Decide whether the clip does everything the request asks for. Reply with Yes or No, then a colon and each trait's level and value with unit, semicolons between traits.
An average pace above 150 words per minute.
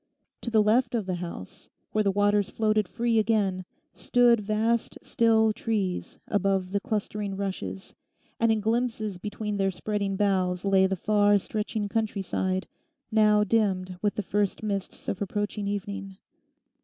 No: average, 145 wpm